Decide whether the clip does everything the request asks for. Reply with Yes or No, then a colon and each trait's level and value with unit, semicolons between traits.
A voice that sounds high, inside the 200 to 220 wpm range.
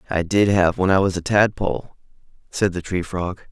No: very low, 90 Hz; fast, 205 wpm